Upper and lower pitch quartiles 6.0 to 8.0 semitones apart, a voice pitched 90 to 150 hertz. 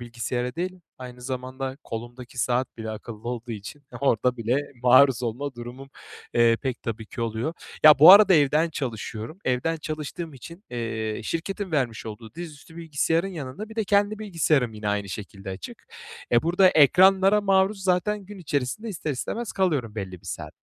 Yes: wide, 6.6 semitones; low, 135 Hz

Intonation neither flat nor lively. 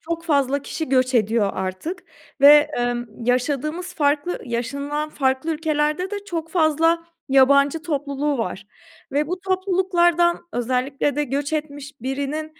Yes: average, 3.9 semitones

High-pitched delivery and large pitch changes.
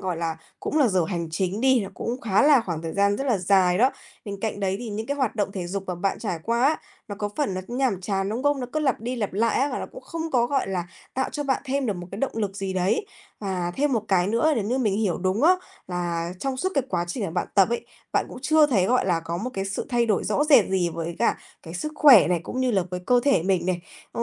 Yes: high, 205 Hz; wide, 5.8 semitones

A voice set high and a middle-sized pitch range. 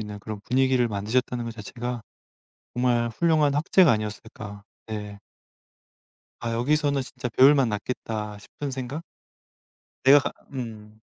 No: low, 120 Hz; average, 3.7 semitones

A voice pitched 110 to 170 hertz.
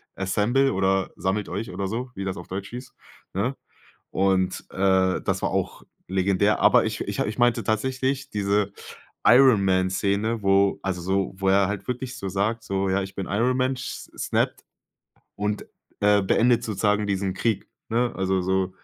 No: low, 100 Hz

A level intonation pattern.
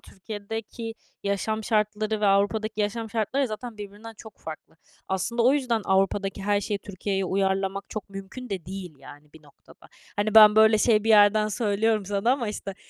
Yes: narrow, 2.0 semitones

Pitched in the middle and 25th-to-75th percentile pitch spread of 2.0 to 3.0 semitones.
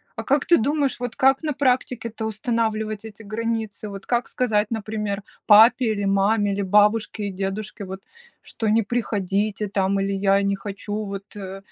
No: high, 210 Hz; narrow, 2.4 semitones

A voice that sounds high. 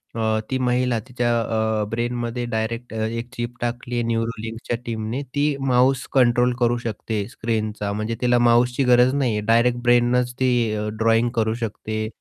No: low, 120 Hz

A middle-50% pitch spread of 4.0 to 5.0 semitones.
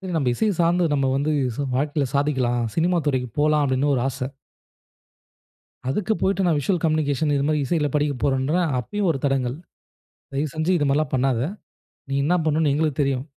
No: average, 2.7 semitones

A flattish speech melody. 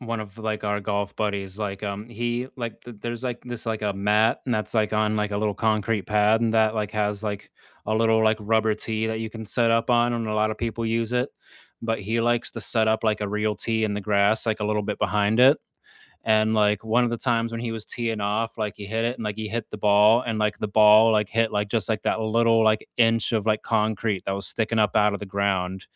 Yes: narrow, 1.6 semitones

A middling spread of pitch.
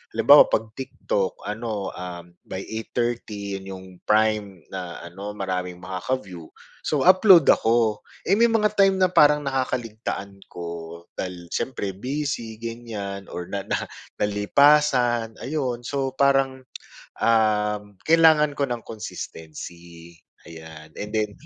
No: wide, 5.8 semitones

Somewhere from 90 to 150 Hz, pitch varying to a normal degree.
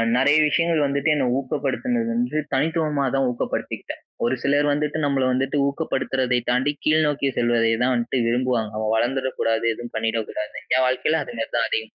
Yes: low, 135 Hz; average, 3.6 semitones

